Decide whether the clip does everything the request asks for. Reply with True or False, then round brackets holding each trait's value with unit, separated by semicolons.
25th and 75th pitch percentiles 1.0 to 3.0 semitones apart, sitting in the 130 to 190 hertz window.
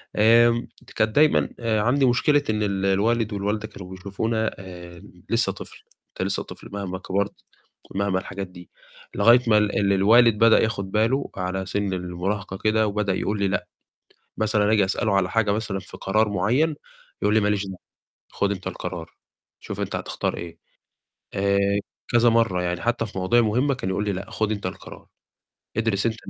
False (2.7 semitones; 105 Hz)